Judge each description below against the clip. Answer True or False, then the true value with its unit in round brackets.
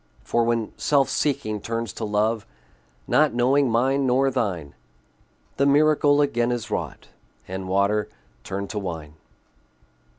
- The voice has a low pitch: True (115 Hz)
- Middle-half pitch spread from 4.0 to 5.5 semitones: True (4.8 semitones)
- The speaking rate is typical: False (130 wpm)